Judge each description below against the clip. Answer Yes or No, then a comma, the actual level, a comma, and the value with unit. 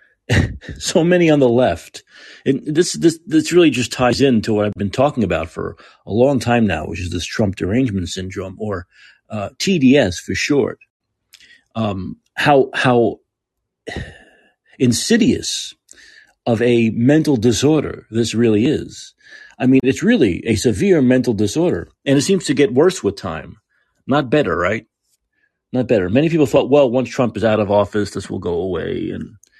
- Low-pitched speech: Yes, low, 125 Hz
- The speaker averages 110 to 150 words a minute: No, average, 165 wpm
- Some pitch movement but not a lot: No, wide, 6.4 semitones